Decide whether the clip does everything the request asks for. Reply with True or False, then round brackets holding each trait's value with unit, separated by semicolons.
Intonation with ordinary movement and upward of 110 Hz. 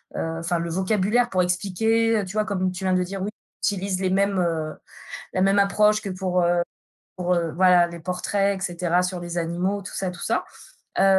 False (2.1 semitones; 185 Hz)